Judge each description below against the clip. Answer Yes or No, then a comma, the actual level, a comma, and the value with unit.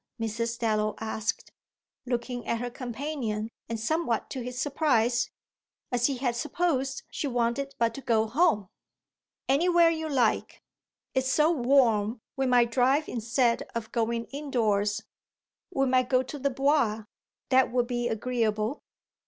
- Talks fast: No, average, 140 wpm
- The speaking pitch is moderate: No, high, 245 Hz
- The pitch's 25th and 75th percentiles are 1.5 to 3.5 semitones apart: Yes, average, 3.1 semitones